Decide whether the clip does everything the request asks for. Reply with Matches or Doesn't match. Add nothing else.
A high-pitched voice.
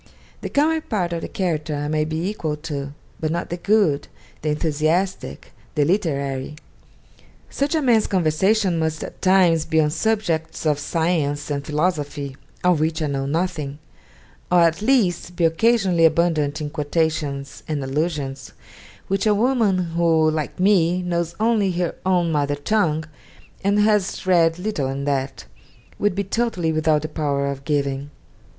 Doesn't match